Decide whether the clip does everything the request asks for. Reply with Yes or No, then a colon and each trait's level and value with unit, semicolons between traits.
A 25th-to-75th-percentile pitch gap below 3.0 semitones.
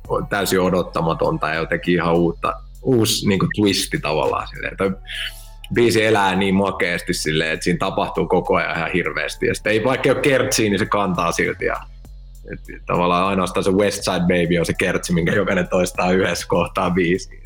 No: average, 3.8 semitones